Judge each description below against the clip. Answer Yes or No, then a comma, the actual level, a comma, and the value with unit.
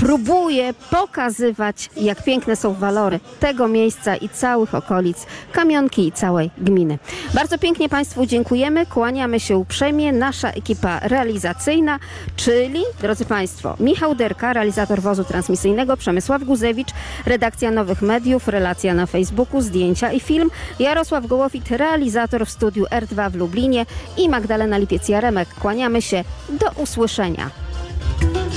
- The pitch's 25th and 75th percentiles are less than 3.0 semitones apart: No, average, 5.1 semitones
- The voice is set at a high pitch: Yes, high, 235 Hz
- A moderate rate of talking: Yes, average, 125 wpm